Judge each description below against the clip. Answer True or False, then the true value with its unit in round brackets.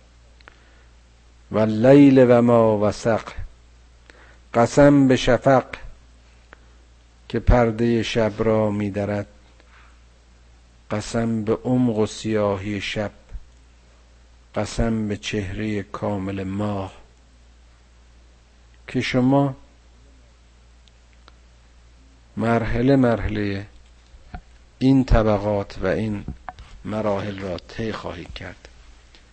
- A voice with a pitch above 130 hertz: False (95 Hz)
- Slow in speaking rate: True (80 wpm)